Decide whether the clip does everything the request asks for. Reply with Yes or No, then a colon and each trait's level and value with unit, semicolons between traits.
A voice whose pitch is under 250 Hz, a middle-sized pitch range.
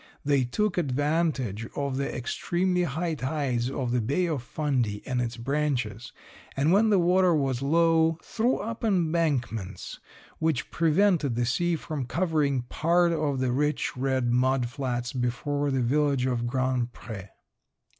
Yes: medium, 140 Hz; average, 4.8 semitones